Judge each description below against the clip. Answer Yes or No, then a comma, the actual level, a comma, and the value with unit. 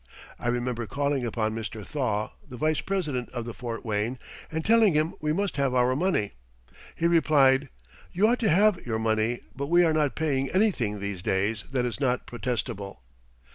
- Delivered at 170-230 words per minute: Yes, average, 180 wpm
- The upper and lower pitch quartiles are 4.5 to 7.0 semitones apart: Yes, wide, 5.6 semitones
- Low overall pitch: Yes, low, 130 Hz